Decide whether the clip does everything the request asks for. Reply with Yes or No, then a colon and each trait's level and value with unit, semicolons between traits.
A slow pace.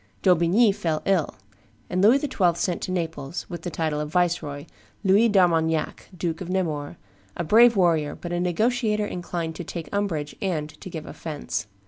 No: average, 165 wpm